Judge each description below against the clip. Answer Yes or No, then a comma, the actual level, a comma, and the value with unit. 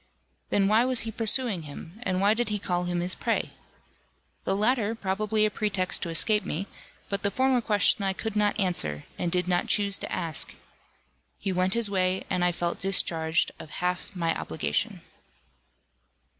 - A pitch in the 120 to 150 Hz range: No, high, 195 Hz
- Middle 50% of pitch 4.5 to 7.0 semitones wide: No, average, 3.2 semitones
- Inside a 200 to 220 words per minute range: No, average, 175 wpm